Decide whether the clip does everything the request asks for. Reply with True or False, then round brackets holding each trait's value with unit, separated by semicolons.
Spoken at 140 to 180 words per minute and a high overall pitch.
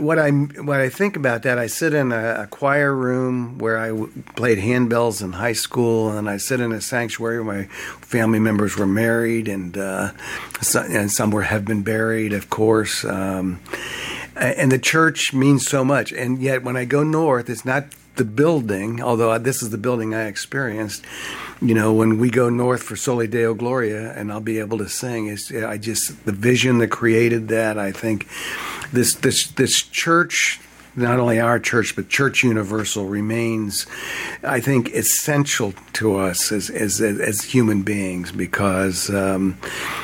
False (175 wpm; 115 Hz)